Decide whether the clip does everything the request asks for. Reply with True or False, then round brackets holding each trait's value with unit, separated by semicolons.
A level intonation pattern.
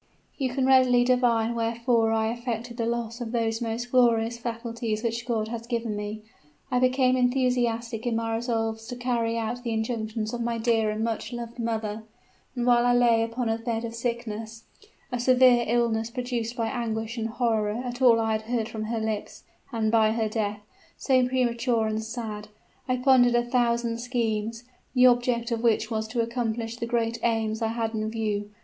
True (1.5 semitones)